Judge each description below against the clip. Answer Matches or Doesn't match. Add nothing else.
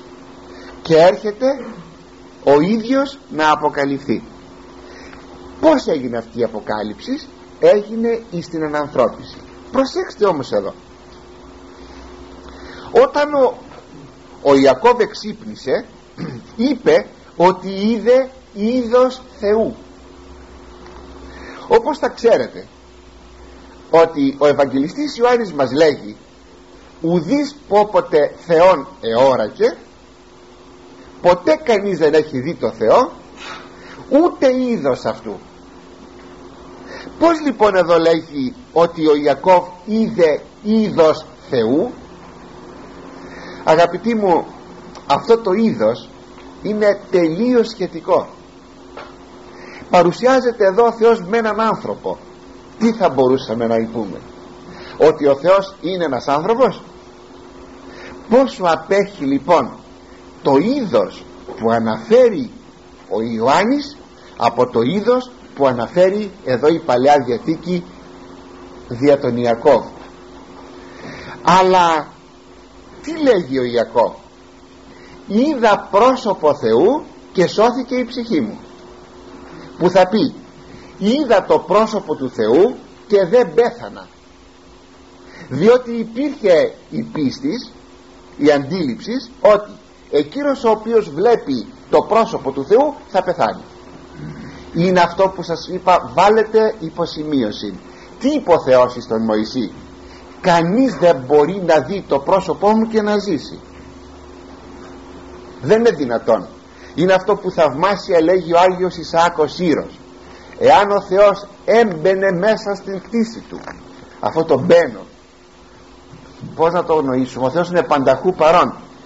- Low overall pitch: Doesn't match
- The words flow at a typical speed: Doesn't match